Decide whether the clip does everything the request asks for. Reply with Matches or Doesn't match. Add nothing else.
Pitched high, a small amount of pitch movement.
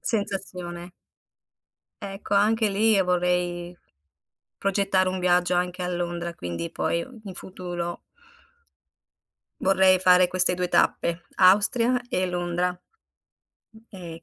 Doesn't match